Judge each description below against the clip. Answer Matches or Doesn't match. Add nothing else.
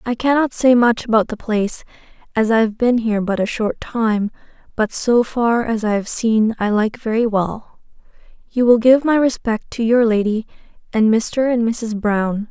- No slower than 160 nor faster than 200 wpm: Matches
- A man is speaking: Doesn't match